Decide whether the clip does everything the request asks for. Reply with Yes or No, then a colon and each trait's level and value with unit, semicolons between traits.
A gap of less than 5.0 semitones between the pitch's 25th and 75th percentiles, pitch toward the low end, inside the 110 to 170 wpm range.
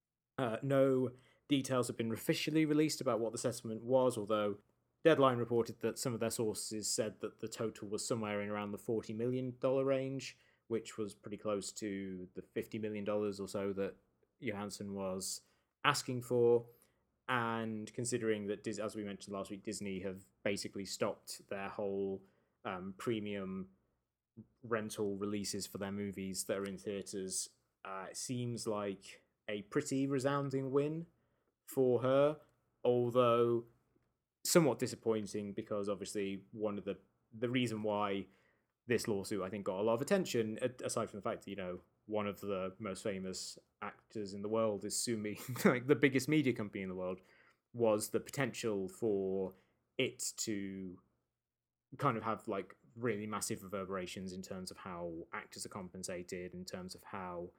Yes: average, 3.7 semitones; low, 110 Hz; average, 160 wpm